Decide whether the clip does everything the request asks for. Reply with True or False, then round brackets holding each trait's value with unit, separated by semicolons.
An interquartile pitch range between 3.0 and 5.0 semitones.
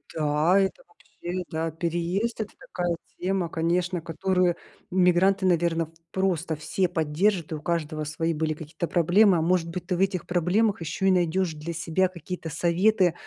False (2.4 semitones)